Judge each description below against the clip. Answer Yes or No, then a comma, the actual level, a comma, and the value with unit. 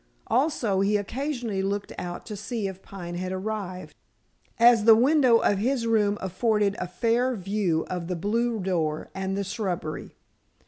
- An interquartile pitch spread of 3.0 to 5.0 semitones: Yes, average, 3.7 semitones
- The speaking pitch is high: Yes, high, 205 Hz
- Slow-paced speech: No, average, 155 wpm